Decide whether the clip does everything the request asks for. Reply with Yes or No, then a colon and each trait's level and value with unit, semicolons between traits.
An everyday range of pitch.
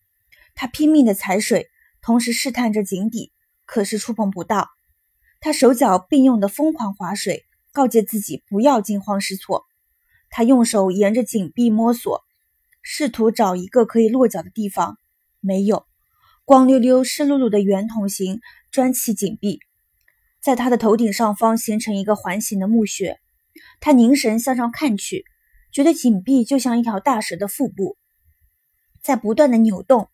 Yes: average, 4.6 semitones